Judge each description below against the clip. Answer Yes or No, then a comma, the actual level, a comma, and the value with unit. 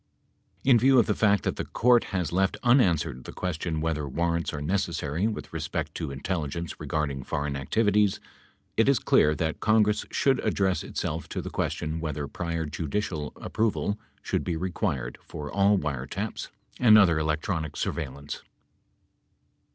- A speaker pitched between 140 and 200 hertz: No, very low, 85 Hz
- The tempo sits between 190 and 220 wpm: No, average, 150 wpm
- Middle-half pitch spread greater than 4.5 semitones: Yes, average, 5.2 semitones